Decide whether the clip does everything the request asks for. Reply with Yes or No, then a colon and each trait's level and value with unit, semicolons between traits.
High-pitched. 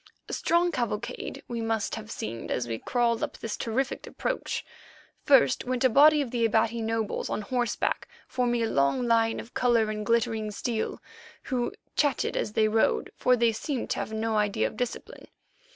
Yes: high, 230 Hz